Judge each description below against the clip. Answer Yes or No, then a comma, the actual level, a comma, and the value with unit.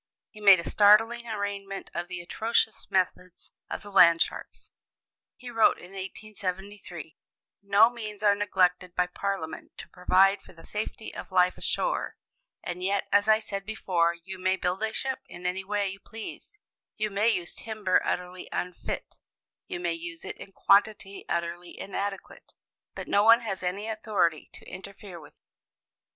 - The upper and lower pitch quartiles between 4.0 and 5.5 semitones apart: No, average, 2.7 semitones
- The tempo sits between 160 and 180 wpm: Yes, average, 165 wpm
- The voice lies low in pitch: No, high, 195 Hz